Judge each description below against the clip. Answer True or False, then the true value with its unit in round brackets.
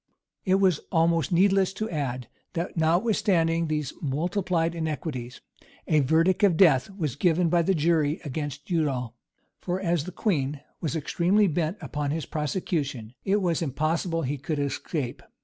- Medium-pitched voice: True (165 Hz)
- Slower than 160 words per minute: True (150 wpm)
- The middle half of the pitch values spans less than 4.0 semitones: True (3.4 semitones)